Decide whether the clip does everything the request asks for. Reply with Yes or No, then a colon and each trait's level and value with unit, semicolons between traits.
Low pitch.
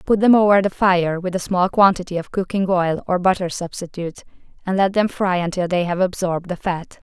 No: medium, 185 Hz